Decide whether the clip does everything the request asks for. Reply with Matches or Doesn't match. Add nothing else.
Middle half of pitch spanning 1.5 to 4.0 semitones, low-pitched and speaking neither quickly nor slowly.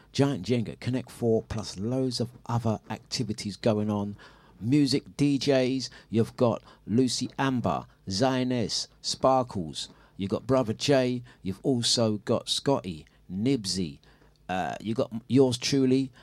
Doesn't match